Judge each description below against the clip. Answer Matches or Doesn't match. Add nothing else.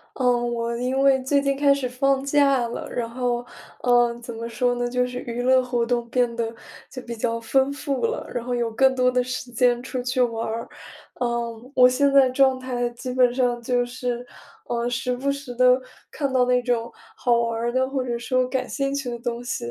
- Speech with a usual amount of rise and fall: Doesn't match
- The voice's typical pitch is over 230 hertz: Matches